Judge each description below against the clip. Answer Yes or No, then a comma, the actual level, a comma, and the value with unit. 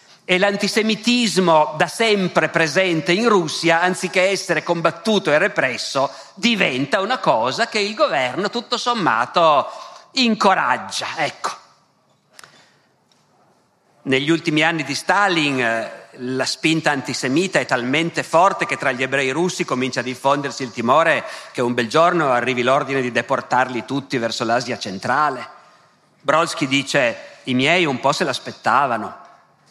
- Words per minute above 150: No, average, 125 wpm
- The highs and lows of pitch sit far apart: Yes, wide, 6.9 semitones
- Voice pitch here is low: No, medium, 165 Hz